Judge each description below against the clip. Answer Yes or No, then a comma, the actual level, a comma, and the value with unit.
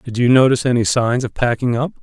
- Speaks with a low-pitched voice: Yes, low, 120 Hz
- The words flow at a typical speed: No, fast, 235 wpm